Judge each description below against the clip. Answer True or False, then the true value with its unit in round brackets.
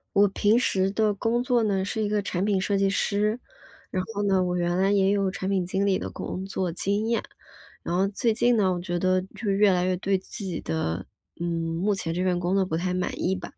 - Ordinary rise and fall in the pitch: False (2.1 semitones)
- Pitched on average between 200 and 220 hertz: False (190 Hz)